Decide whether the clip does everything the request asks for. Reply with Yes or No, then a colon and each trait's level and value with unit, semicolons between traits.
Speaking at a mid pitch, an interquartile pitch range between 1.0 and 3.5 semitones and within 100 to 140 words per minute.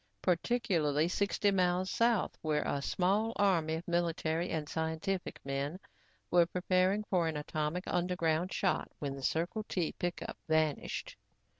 Yes: medium, 175 Hz; average, 2.8 semitones; slow, 135 wpm